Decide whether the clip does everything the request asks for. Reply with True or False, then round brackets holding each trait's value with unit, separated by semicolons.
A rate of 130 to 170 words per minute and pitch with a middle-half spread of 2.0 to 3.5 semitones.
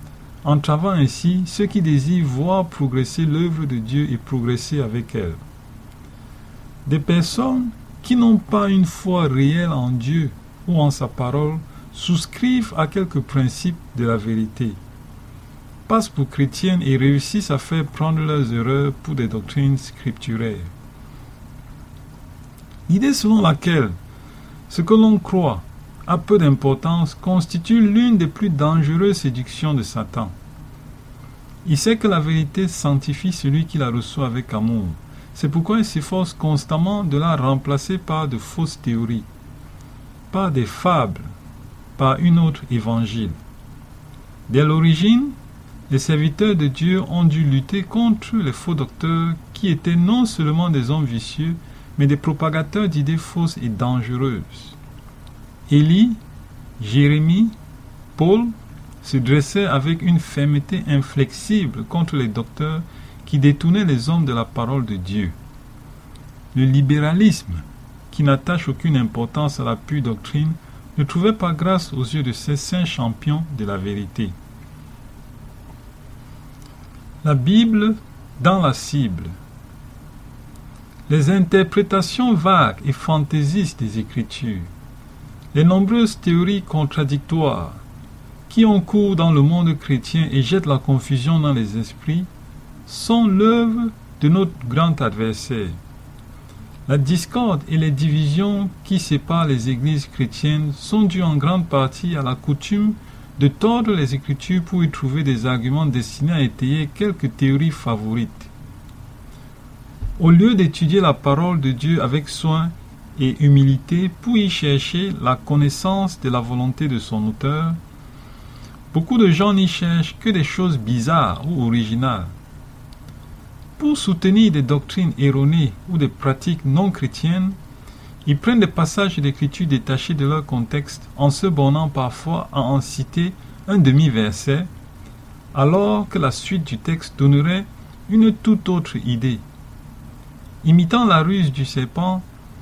False (135 wpm; 5.2 semitones)